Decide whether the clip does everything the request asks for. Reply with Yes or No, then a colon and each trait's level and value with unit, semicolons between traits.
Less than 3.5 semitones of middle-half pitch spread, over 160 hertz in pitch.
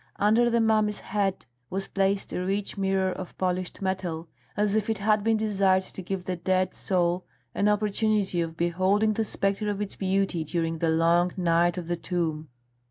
Yes: average, 2.9 semitones; high, 190 Hz